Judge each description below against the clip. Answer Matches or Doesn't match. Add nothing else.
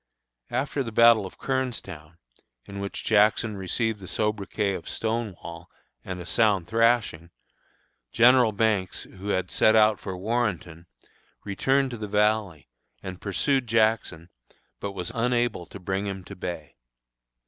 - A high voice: Doesn't match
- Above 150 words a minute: Doesn't match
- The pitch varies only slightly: Doesn't match